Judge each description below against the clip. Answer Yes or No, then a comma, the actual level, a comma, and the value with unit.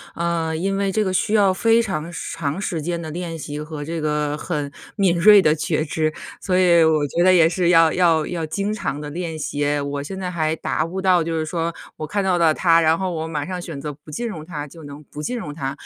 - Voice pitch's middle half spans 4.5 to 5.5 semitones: No, average, 3.0 semitones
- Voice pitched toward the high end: No, medium, 165 Hz